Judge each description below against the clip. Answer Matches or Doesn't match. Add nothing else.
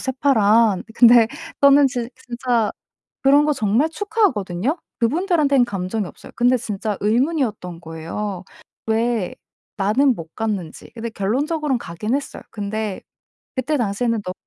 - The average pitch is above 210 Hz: Matches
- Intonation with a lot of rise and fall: Doesn't match